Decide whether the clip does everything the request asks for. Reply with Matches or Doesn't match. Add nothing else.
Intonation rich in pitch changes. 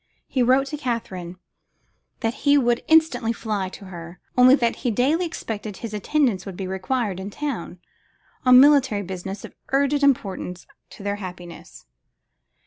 Matches